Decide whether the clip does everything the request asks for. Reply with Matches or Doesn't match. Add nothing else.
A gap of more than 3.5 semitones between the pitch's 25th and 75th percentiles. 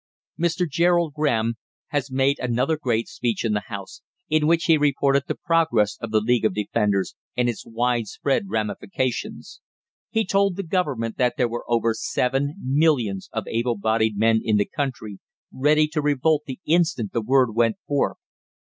Matches